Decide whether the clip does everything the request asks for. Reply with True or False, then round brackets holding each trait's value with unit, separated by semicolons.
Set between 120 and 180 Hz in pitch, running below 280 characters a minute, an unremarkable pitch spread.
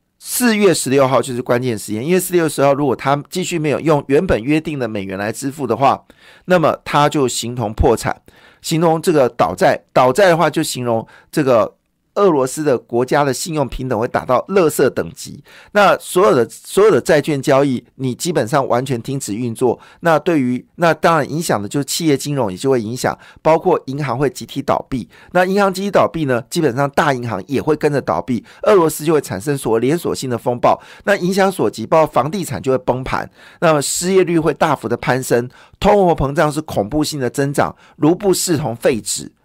False (140 Hz; 310 characters per minute; 4.7 semitones)